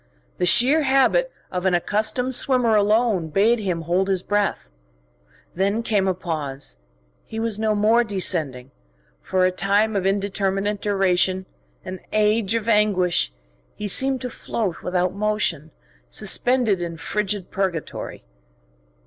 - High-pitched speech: Yes, high, 200 Hz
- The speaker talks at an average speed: No, slow, 130 wpm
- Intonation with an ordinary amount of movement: Yes, average, 3.3 semitones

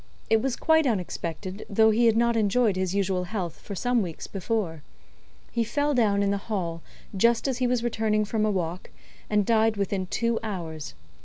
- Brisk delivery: No, average, 185 wpm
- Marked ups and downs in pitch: No, average, 3.7 semitones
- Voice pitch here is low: No, high, 210 Hz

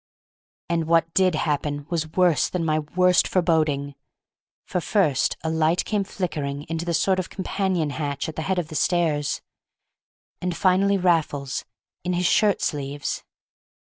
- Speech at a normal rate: Yes, average, 150 wpm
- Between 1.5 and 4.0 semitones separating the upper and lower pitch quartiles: Yes, average, 3.3 semitones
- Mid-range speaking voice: Yes, medium, 165 Hz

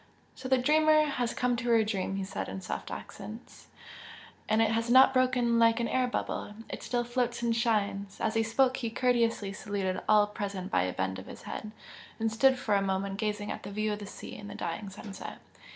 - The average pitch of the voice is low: No, high, 220 Hz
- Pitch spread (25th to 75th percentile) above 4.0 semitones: No, average, 3.3 semitones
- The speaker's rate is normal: No, fast, 215 wpm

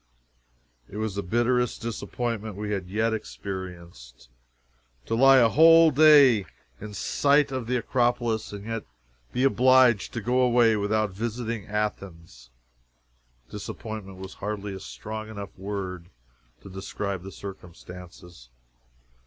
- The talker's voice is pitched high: No, low, 105 Hz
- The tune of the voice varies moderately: Yes, average, 3.8 semitones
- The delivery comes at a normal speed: No, slow, 125 wpm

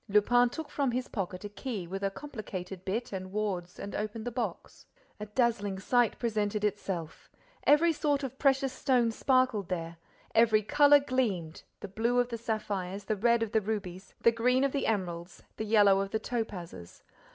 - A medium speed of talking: Yes, average, 180 wpm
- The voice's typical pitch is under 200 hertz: No, high, 215 Hz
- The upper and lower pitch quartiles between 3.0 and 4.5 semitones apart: Yes, average, 4.1 semitones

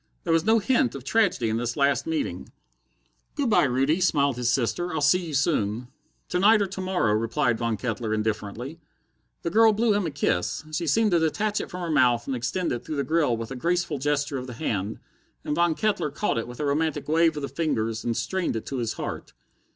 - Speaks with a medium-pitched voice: Yes, medium, 145 Hz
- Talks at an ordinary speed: No, fast, 225 wpm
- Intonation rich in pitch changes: Yes, wide, 6.7 semitones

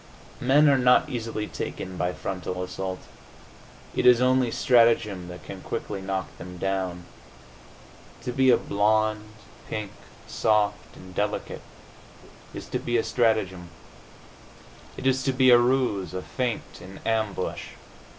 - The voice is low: Yes, low, 110 Hz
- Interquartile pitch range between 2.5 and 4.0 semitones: No, average, 4.8 semitones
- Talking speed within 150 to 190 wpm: No, slow, 135 wpm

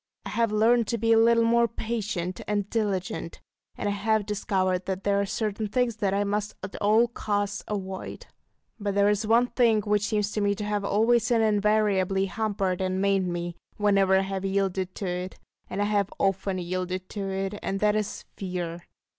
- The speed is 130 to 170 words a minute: No, average, 195 wpm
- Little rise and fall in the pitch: Yes, narrow, 2.1 semitones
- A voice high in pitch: Yes, high, 205 Hz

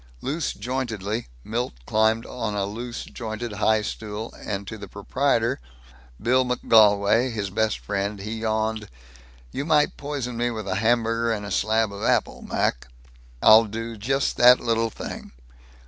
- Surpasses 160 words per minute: No, average, 145 wpm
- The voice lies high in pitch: No, low, 110 Hz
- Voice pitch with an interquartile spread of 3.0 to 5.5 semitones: No, narrow, 2.4 semitones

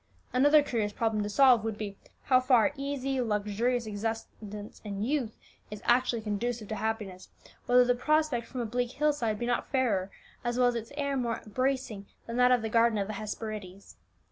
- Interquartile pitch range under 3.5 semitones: Yes, average, 3.0 semitones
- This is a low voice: No, high, 235 Hz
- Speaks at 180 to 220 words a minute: Yes, average, 190 wpm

